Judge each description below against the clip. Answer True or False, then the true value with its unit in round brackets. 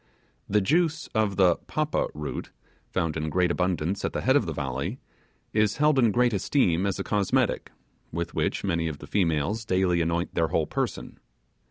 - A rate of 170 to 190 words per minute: True (180 wpm)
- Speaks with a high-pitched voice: False (95 Hz)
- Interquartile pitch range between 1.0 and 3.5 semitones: False (4.8 semitones)